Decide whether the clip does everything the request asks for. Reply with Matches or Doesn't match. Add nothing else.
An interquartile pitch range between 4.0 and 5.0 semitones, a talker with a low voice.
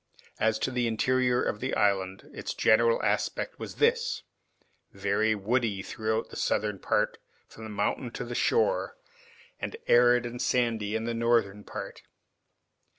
Doesn't match